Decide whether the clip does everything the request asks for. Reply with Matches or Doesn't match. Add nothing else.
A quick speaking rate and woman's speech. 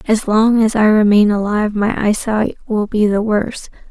Doesn't match